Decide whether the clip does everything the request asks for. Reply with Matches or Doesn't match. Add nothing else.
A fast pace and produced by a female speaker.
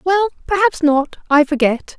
Doesn't match